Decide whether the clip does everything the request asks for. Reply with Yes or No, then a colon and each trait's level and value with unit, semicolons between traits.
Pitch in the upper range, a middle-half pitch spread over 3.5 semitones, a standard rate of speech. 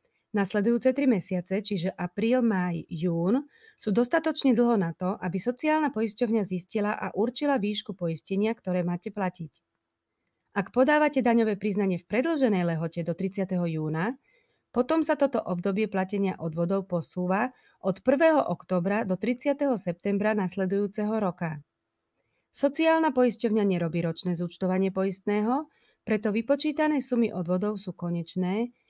Yes: high, 205 Hz; wide, 5.4 semitones; average, 125 wpm